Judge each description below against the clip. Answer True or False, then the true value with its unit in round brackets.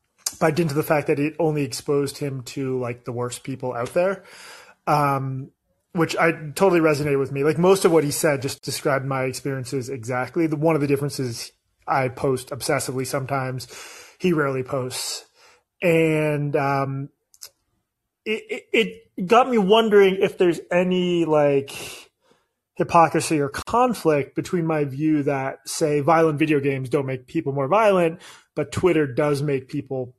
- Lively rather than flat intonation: False (3.8 semitones)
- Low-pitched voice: False (150 Hz)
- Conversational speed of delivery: True (160 wpm)